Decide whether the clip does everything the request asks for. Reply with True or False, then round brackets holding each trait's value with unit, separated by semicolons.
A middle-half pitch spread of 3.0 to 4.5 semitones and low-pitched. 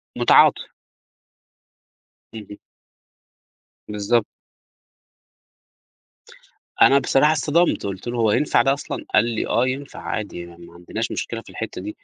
False (4.9 semitones; 115 Hz)